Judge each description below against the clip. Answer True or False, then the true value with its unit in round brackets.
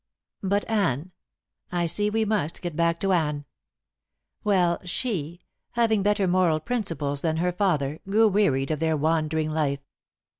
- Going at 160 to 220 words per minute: False (145 wpm)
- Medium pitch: True (170 Hz)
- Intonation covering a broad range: False (4.5 semitones)